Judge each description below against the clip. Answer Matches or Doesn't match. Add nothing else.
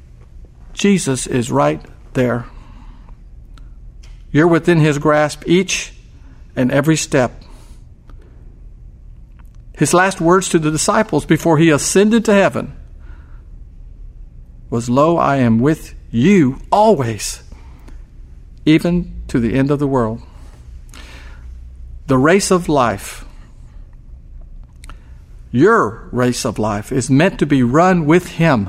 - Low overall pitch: Matches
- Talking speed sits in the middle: Doesn't match